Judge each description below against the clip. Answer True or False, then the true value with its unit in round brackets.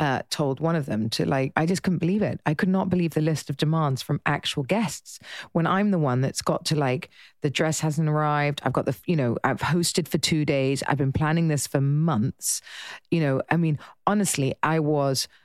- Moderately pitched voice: True (155 Hz)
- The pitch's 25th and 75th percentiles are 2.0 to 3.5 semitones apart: True (2.8 semitones)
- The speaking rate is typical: False (225 wpm)